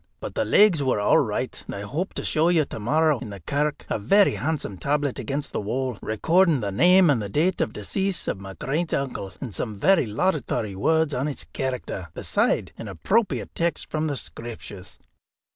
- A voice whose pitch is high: No, medium, 140 Hz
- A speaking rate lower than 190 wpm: No, average, 195 wpm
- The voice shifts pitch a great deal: Yes, wide, 7.3 semitones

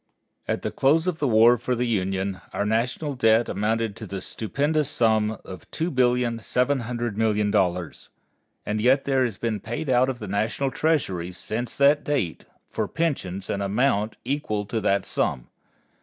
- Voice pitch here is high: No, low, 115 Hz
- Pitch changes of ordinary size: Yes, average, 4.3 semitones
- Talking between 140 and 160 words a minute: Yes, average, 155 wpm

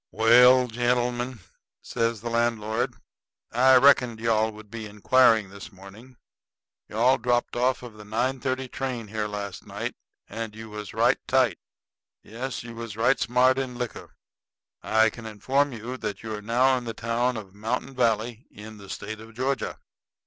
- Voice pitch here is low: Yes, low, 115 Hz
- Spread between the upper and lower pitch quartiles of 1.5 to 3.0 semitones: Yes, narrow, 2.4 semitones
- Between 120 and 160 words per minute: No, average, 170 wpm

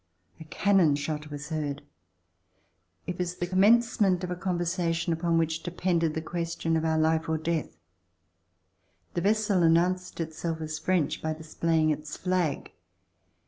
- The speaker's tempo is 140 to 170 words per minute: Yes, average, 145 wpm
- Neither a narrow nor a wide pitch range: No, narrow, 2.2 semitones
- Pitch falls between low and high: Yes, medium, 165 Hz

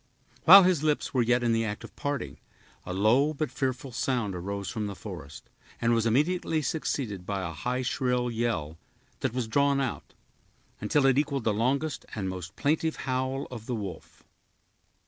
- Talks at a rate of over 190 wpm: No, average, 175 wpm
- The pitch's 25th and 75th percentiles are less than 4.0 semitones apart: No, average, 5.0 semitones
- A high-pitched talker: No, low, 125 Hz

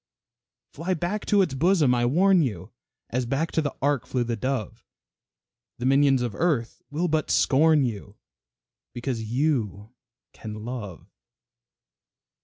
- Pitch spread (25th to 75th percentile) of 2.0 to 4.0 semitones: No, average, 5.1 semitones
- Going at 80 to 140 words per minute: Yes, slow, 135 wpm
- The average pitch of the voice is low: Yes, low, 130 Hz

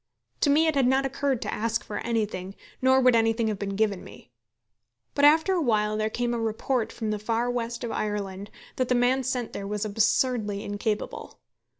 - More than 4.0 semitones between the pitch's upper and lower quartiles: No, average, 3.4 semitones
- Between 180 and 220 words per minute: Yes, average, 200 wpm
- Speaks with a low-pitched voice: No, high, 230 Hz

